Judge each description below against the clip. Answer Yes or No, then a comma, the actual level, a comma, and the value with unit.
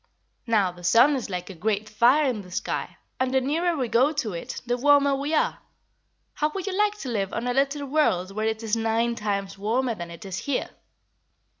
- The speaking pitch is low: No, high, 235 Hz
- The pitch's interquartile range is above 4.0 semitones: Yes, wide, 5.5 semitones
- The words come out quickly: Yes, fast, 215 wpm